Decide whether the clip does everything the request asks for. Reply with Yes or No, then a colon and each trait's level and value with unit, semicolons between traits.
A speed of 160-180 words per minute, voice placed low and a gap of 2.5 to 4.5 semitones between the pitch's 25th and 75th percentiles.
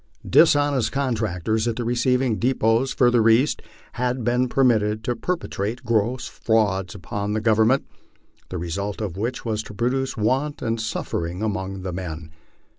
No: average, 150 wpm; low, 115 Hz; average, 3.4 semitones